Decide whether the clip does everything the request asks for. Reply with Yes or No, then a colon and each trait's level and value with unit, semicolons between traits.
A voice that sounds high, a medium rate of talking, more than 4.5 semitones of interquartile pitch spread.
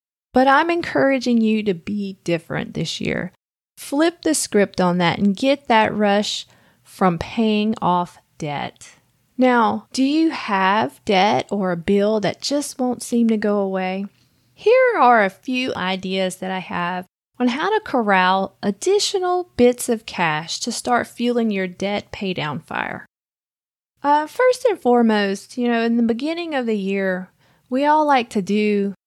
Yes: high, 220 Hz; average, 160 wpm; wide, 5.4 semitones